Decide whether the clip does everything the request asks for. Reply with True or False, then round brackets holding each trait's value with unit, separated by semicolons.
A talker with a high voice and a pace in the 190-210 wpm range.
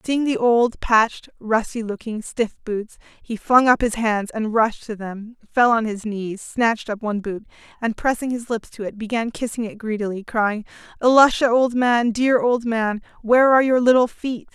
True (230 Hz; 195 wpm)